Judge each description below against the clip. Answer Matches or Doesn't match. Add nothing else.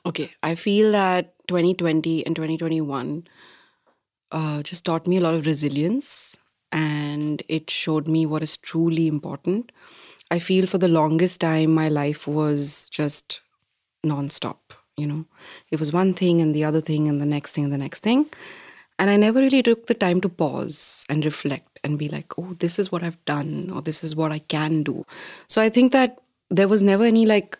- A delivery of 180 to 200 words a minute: Matches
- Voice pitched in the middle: Matches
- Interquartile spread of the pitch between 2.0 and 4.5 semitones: Matches